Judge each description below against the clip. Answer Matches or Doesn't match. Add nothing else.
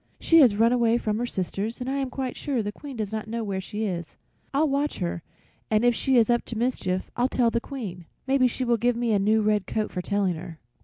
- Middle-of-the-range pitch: Doesn't match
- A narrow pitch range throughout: Doesn't match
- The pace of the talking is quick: Matches